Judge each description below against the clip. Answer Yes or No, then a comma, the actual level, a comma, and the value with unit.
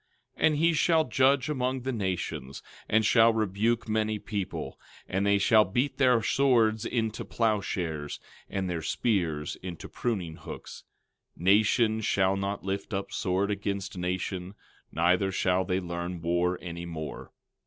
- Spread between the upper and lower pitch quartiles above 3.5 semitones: Yes, average, 3.9 semitones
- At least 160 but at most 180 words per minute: No, average, 145 wpm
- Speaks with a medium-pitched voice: No, low, 100 Hz